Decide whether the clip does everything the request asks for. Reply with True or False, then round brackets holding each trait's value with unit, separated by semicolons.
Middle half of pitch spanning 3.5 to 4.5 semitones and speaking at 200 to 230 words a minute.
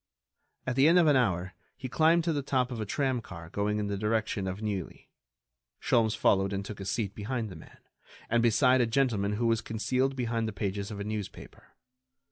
True (4.1 semitones; 205 wpm)